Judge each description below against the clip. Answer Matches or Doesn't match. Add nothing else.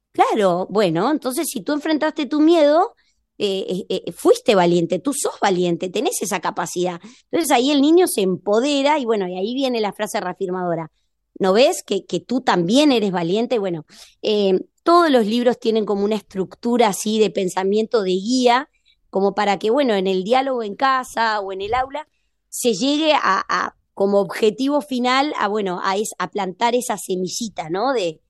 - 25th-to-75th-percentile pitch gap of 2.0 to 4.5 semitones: Doesn't match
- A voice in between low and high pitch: Doesn't match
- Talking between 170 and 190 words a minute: Matches